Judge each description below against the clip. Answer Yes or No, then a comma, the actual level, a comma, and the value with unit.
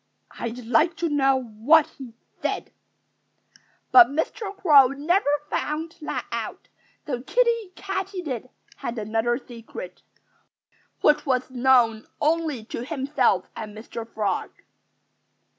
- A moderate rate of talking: No, slow, 110 wpm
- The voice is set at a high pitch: Yes, very high, 270 Hz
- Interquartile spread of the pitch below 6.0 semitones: Yes, wide, 5.6 semitones